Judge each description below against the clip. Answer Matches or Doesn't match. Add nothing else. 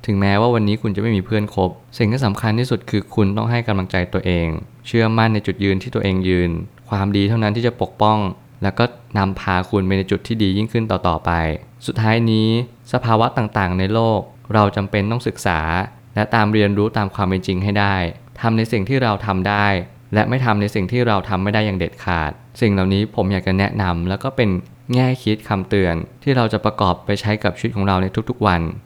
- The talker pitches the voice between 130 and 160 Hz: Doesn't match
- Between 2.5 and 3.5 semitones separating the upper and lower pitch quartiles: Matches